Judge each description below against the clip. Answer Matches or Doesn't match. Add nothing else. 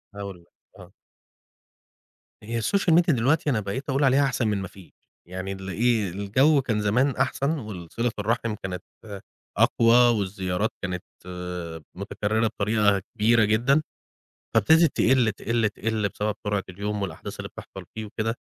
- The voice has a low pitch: Matches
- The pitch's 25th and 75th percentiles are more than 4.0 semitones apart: Doesn't match